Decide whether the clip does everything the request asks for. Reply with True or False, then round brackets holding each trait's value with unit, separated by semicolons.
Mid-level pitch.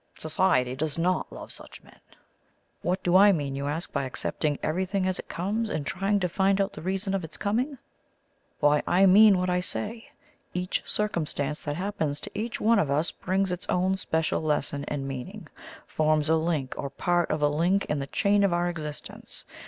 True (175 Hz)